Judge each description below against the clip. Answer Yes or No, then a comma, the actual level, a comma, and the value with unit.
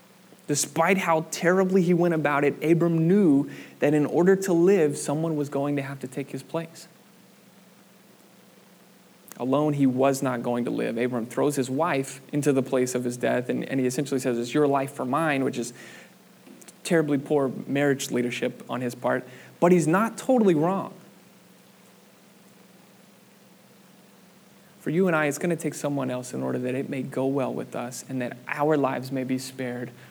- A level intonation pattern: No, average, 4.7 semitones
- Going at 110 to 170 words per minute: No, average, 180 wpm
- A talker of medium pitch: Yes, medium, 145 Hz